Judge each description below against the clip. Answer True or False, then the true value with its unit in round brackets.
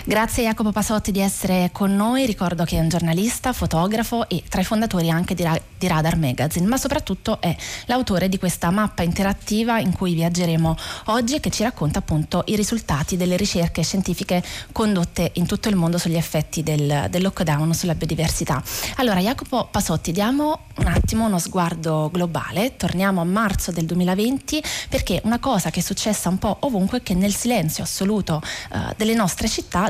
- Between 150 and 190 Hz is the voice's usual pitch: True (185 Hz)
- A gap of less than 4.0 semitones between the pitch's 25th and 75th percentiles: False (4.3 semitones)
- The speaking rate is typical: False (175 wpm)